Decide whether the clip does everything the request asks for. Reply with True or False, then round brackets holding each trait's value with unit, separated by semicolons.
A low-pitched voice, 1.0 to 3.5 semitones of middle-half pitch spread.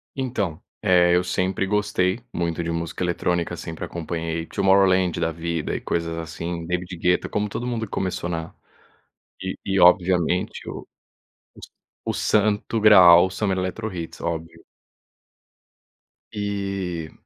True (90 Hz; 2.7 semitones)